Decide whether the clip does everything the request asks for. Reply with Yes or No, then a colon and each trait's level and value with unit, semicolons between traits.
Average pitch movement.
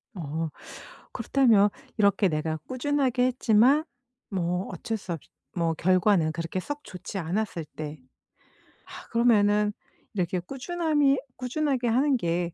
No: wide, 6.7 semitones